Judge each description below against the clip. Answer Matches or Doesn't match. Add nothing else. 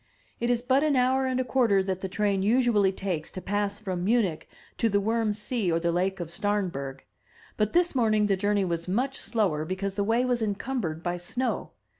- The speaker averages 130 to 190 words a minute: Doesn't match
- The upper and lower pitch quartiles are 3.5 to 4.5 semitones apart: Matches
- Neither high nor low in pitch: Doesn't match